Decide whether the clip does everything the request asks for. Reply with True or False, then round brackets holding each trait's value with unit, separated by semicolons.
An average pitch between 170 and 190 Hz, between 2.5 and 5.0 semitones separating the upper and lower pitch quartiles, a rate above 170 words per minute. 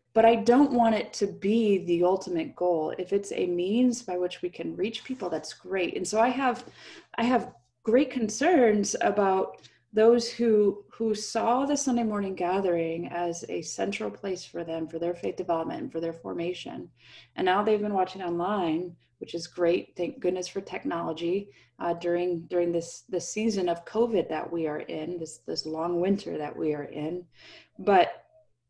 True (185 Hz; 4.6 semitones; 180 wpm)